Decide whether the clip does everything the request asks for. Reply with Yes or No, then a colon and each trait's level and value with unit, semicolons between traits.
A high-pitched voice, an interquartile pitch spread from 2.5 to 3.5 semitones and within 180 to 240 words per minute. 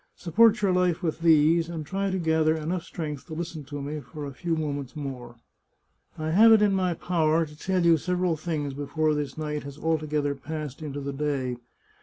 No: medium, 155 Hz; average, 2.8 semitones; average, 200 wpm